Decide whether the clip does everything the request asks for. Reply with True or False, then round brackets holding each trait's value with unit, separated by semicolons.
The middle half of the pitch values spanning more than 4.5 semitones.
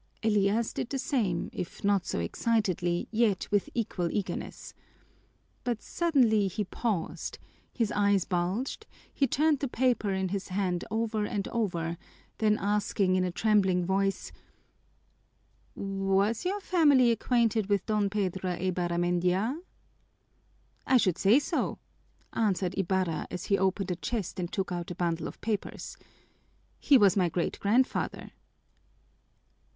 False (3.7 semitones)